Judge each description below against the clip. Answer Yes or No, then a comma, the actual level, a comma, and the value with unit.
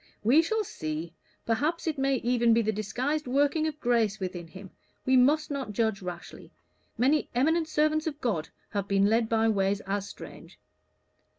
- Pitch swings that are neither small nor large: No, wide, 6.7 semitones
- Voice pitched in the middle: No, high, 235 Hz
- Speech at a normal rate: Yes, average, 170 wpm